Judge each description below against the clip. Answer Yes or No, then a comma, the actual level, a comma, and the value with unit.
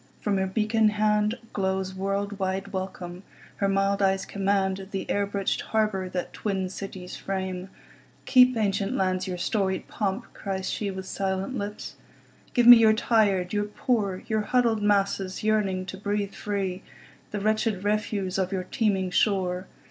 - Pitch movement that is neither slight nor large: No, narrow, 1.8 semitones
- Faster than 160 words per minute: No, slow, 135 wpm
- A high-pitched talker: Yes, high, 195 Hz